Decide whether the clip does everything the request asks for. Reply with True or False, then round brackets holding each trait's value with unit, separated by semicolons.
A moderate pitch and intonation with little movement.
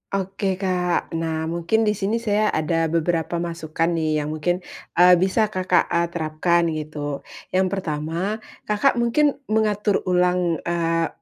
False (175 Hz; 3.0 semitones)